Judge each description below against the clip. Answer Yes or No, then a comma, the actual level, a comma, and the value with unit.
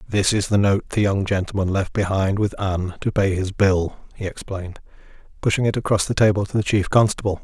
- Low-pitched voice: Yes, low, 100 Hz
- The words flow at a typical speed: No, fast, 210 wpm